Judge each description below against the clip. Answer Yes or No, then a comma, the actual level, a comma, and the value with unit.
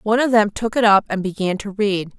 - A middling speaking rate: No, fast, 275 wpm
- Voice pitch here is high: Yes, high, 205 Hz